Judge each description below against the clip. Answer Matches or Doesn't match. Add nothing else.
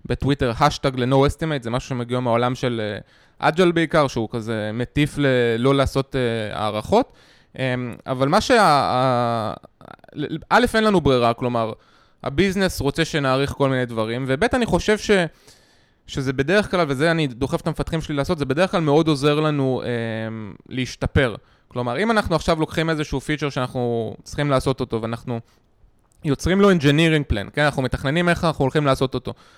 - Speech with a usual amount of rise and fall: Matches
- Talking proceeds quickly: Matches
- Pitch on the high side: Doesn't match